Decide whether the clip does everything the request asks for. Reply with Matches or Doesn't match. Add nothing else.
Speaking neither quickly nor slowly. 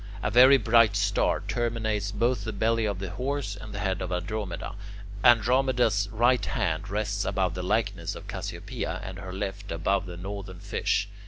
Matches